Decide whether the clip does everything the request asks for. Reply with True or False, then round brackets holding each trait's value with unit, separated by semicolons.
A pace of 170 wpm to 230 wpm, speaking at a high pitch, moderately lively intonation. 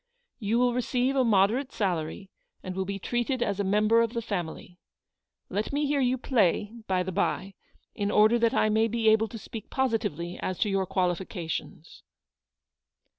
True (175 wpm; 210 Hz; 3.9 semitones)